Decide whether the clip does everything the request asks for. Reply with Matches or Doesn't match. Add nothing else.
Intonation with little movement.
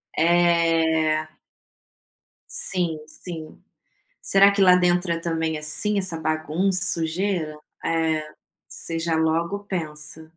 Matches